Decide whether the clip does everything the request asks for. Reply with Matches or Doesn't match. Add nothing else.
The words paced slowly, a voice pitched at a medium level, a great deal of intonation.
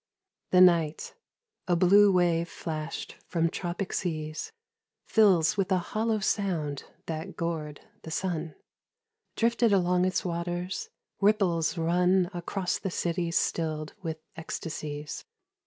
Doesn't match